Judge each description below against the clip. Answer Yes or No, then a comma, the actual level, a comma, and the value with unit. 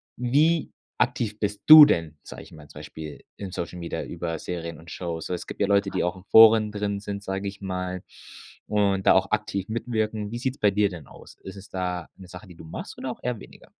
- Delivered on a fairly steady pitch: No, average, 3.2 semitones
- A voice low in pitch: Yes, low, 100 Hz